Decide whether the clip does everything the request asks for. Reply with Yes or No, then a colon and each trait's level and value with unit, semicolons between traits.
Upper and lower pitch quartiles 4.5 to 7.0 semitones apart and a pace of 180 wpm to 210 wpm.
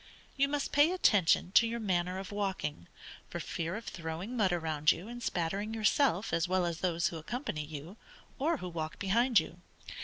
Yes: wide, 5.6 semitones; average, 185 wpm